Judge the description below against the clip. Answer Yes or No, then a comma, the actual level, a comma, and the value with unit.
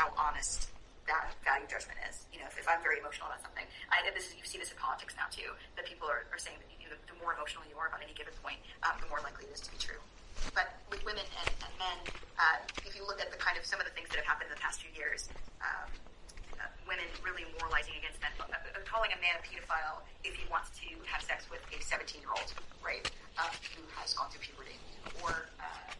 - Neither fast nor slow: No, fast, 260 wpm